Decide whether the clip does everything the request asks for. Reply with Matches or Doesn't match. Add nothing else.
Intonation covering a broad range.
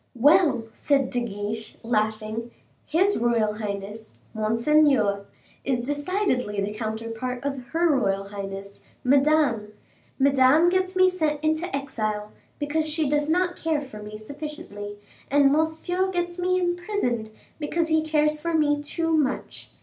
Matches